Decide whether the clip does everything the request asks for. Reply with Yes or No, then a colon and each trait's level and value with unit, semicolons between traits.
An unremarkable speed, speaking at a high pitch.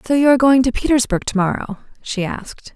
Yes: average, 195 wpm; high, 240 Hz